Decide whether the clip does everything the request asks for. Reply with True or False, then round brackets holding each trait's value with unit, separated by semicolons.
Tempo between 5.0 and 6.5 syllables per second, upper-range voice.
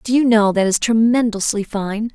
False (4.7 syllables/s; 220 Hz)